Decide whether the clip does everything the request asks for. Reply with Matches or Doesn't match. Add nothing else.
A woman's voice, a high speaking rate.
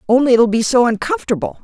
Matches